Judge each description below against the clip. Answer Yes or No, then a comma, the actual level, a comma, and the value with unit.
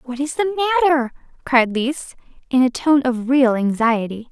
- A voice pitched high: Yes, very high, 265 Hz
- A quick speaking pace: No, average, 165 wpm